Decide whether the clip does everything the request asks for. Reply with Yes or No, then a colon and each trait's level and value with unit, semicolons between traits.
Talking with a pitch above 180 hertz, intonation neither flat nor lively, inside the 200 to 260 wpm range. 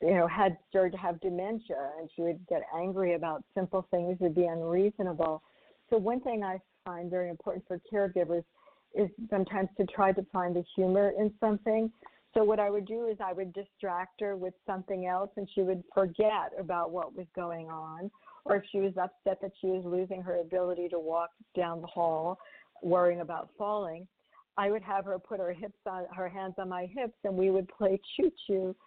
No: high, 190 Hz; narrow, 2.3 semitones; fast, 205 wpm